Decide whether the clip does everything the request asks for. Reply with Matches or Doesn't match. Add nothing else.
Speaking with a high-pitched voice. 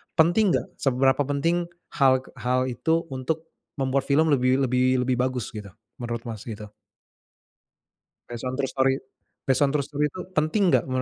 Doesn't match